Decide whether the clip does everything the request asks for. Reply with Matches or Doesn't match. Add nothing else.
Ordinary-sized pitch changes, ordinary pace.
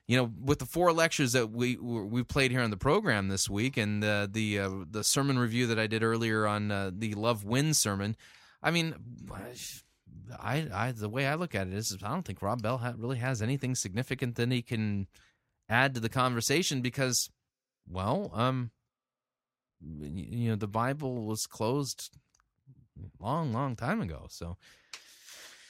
Matches